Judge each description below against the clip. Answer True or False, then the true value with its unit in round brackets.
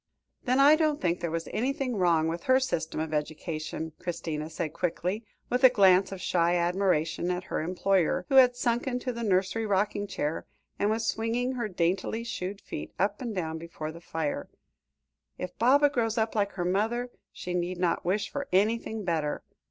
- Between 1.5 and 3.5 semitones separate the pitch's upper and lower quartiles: False (5.5 semitones)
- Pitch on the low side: False (190 Hz)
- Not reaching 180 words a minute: False (185 wpm)